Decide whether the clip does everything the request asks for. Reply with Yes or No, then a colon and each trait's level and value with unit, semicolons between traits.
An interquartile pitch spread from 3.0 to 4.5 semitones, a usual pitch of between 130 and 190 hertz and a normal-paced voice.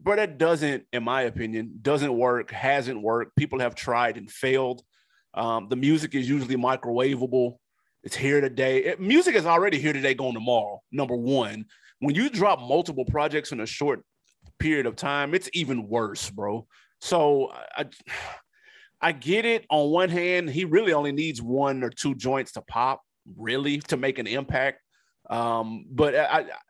Yes: average, 3.7 semitones; low, 135 Hz; average, 170 wpm